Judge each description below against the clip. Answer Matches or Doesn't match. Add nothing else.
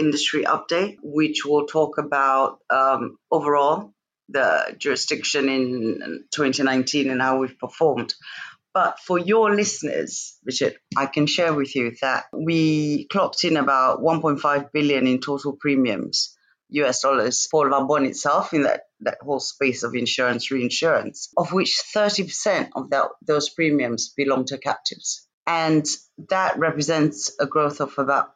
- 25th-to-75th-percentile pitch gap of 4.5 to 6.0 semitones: Doesn't match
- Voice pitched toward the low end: Doesn't match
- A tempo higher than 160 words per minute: Doesn't match